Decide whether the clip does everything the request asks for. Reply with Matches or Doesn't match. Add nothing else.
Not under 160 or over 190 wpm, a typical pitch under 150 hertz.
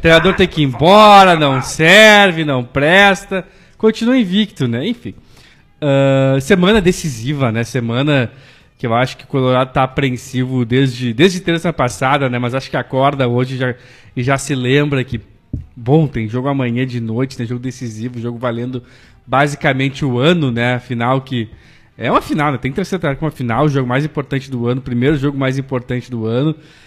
Matches